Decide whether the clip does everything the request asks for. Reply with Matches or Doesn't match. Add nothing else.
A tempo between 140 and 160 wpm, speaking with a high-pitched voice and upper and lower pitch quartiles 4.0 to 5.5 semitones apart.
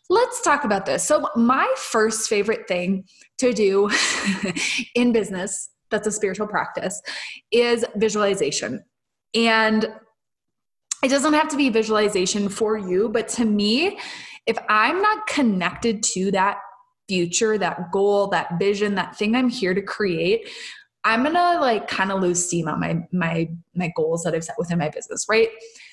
Matches